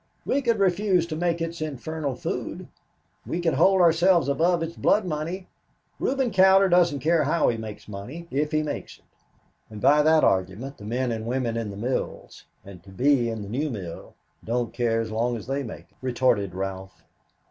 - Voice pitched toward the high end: No, medium, 140 Hz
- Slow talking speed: No, average, 190 wpm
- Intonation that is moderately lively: No, wide, 7.0 semitones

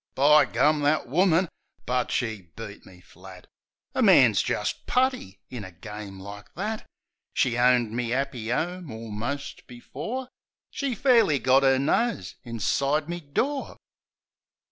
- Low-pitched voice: Yes, low, 130 Hz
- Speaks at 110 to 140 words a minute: Yes, slow, 135 wpm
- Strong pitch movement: Yes, wide, 6.8 semitones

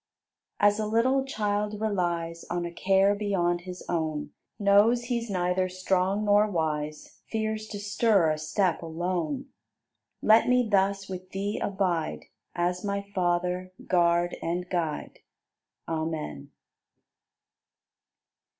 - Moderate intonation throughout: Yes, average, 3.1 semitones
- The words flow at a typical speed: No, slow, 120 wpm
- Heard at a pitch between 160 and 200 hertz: Yes, medium, 185 Hz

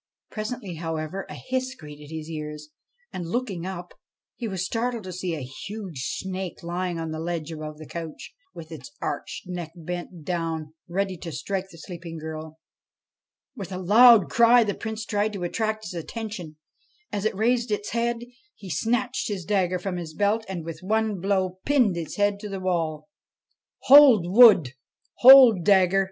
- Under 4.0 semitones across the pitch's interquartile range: No, average, 4.6 semitones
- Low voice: No, medium, 185 Hz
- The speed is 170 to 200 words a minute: Yes, average, 175 wpm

